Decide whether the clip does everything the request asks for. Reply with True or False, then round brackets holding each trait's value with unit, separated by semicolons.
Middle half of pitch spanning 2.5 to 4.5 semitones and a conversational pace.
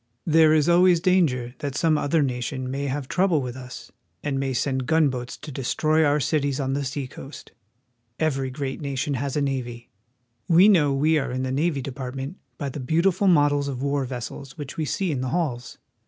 False (3.1 semitones; 210 wpm)